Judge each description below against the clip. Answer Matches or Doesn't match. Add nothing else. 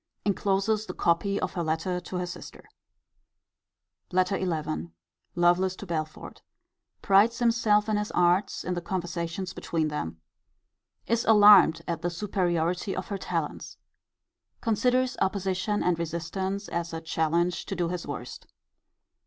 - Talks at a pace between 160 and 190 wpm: Doesn't match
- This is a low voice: Doesn't match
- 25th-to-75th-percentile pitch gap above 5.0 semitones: Doesn't match